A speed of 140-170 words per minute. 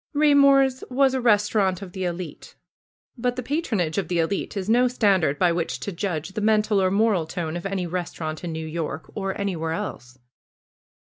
No: average, 190 wpm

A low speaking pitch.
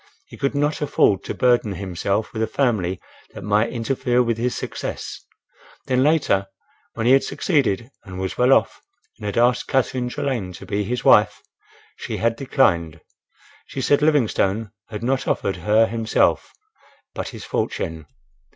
Yes: low, 115 Hz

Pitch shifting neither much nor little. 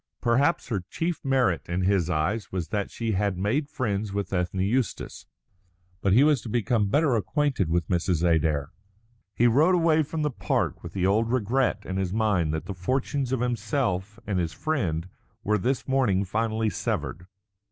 No: wide, 5.9 semitones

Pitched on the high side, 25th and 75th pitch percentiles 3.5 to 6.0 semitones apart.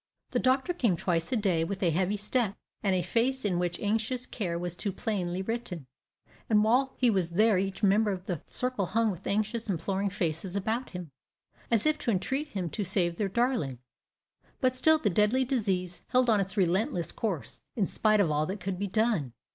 Yes: high, 200 Hz; average, 4.2 semitones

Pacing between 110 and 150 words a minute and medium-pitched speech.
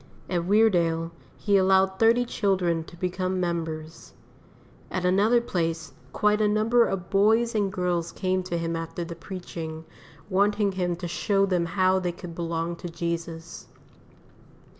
Yes: average, 145 wpm; medium, 180 Hz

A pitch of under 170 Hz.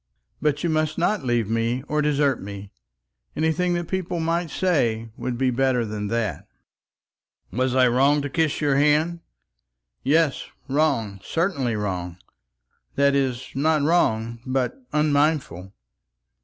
Yes: low, 135 Hz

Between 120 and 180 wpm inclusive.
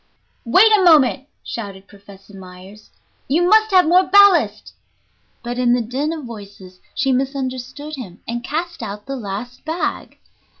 Yes: average, 145 wpm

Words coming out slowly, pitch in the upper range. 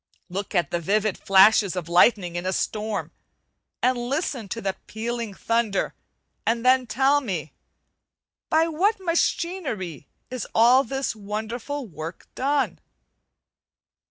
Yes: slow, 125 wpm; high, 225 Hz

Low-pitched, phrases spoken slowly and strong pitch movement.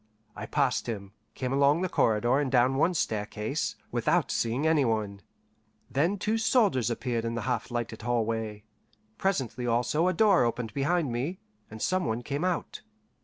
No: low, 125 Hz; average, 165 wpm; wide, 5.8 semitones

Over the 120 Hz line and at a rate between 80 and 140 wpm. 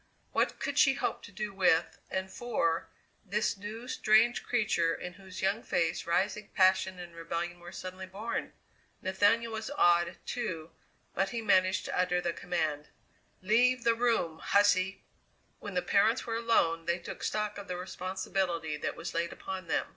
No: high, 190 Hz; average, 165 wpm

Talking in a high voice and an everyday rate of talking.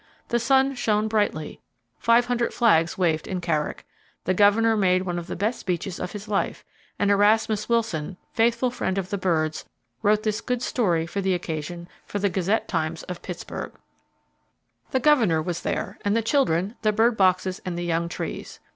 Yes: high, 200 Hz; average, 175 wpm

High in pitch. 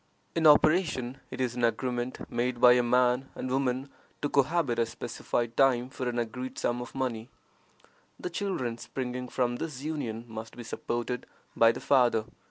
No: low, 125 Hz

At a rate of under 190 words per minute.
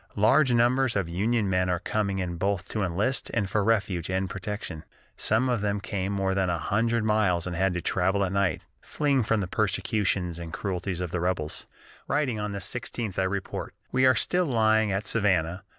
No: average, 200 wpm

